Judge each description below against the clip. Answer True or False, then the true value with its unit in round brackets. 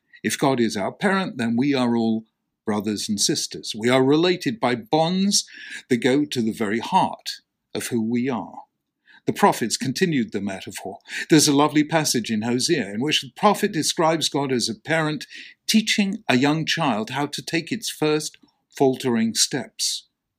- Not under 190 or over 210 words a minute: False (170 wpm)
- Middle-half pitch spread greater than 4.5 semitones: True (5.2 semitones)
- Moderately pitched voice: True (145 Hz)